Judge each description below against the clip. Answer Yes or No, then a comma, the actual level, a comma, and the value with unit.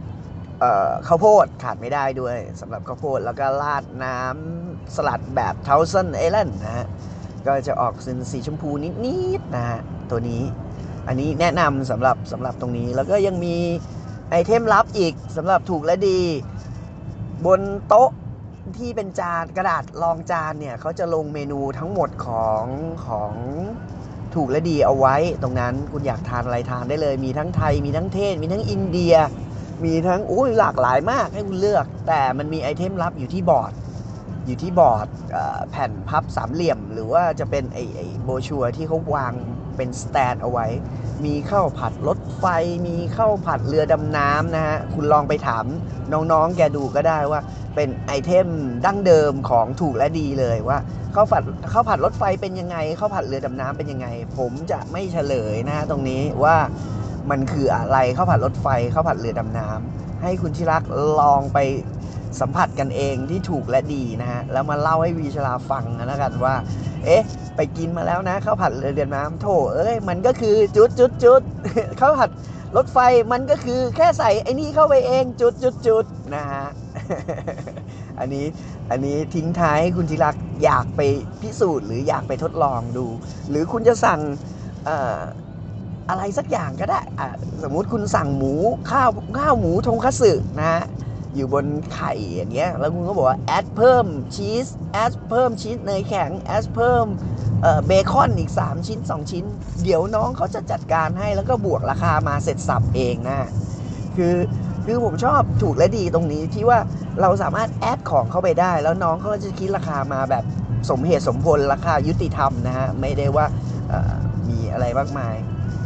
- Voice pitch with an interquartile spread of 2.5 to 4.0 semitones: No, average, 4.9 semitones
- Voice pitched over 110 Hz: Yes, medium, 140 Hz